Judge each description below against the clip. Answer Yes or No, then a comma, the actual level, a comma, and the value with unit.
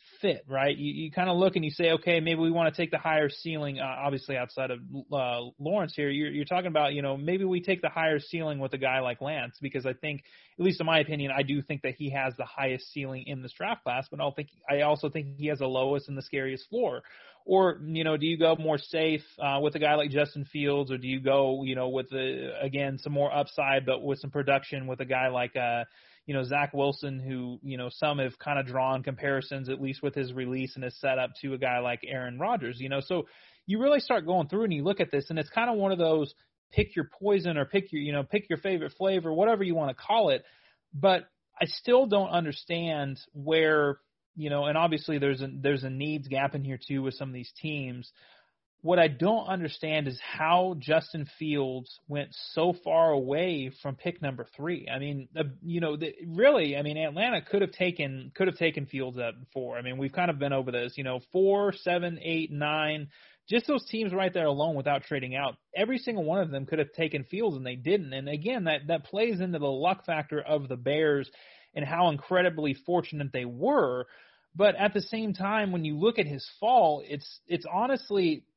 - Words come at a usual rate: No, fast, 230 wpm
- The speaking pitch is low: No, medium, 150 Hz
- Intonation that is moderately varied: Yes, average, 4.0 semitones